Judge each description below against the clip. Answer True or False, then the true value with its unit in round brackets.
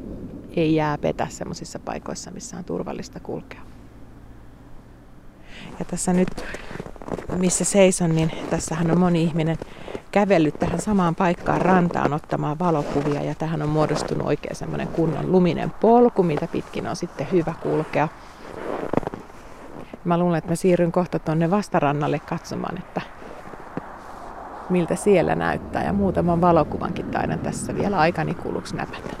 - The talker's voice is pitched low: False (170 Hz)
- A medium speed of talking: True (130 wpm)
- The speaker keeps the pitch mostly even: True (2.3 semitones)